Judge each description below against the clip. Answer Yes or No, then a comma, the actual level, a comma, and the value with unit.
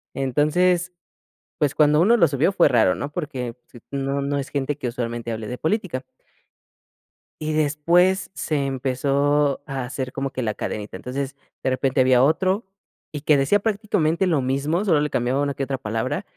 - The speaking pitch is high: No, medium, 140 Hz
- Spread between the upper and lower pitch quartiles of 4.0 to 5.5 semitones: No, average, 3.3 semitones